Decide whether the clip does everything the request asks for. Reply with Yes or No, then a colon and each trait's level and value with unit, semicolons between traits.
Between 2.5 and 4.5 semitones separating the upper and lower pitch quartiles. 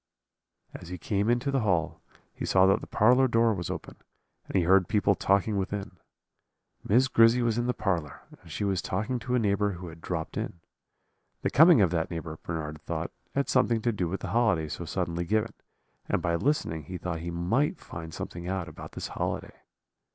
No: average, 5.2 semitones